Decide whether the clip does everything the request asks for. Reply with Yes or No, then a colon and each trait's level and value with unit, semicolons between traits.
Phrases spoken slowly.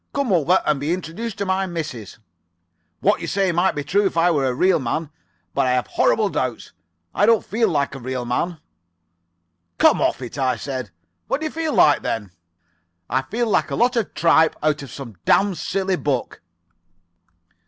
No: average, 190 wpm